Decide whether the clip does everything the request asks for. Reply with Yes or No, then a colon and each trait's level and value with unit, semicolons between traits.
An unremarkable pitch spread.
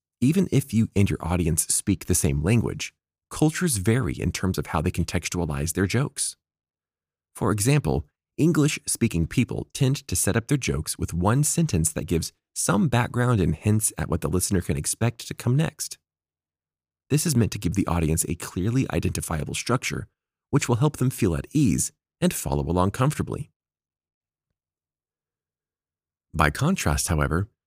No: wide, 7.6 semitones